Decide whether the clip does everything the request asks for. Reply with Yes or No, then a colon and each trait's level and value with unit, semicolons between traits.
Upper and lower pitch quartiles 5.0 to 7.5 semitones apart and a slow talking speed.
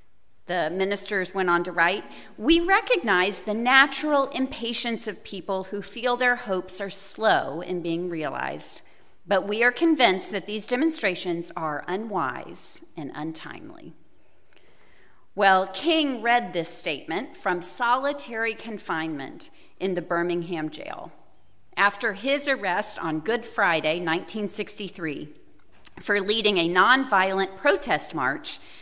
Yes: average, 5.3 semitones; slow, 120 wpm